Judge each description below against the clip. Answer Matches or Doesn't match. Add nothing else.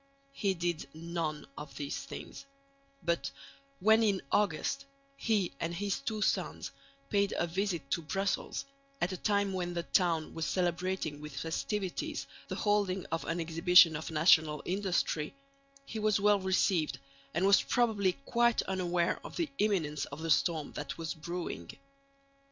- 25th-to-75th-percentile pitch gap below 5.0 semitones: Matches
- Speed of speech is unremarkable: Matches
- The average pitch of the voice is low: Doesn't match